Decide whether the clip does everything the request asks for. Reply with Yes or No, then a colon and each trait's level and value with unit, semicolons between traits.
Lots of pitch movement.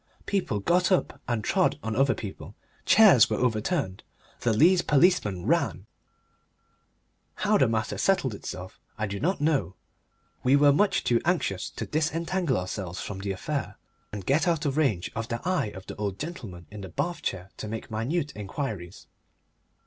Yes: wide, 8.1 semitones